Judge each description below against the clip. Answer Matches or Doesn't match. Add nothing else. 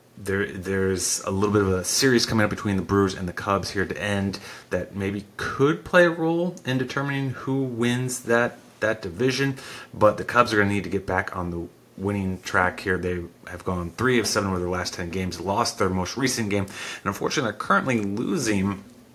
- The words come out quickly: Matches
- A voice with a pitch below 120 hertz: Matches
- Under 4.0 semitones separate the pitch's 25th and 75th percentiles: Doesn't match